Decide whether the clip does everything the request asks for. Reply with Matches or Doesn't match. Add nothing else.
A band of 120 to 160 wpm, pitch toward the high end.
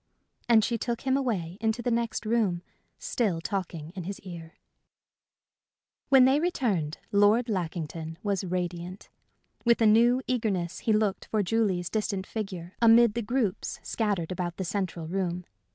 Matches